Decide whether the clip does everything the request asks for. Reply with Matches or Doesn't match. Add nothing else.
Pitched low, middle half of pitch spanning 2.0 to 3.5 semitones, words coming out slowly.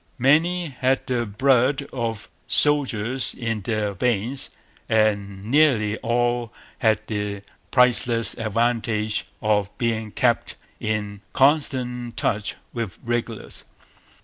Matches